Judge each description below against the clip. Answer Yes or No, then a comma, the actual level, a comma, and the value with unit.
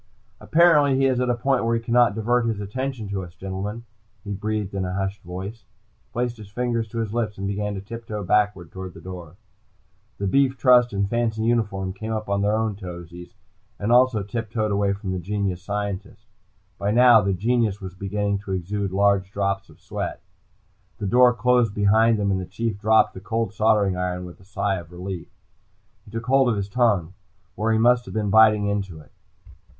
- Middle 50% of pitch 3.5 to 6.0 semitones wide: No, average, 3.0 semitones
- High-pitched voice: No, low, 105 Hz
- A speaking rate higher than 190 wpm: Yes, fast, 205 wpm